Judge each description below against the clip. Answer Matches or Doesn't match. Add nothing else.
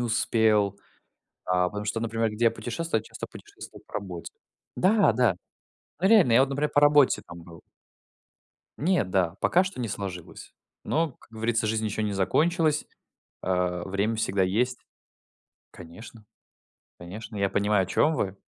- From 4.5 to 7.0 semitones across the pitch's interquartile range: Matches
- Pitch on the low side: Matches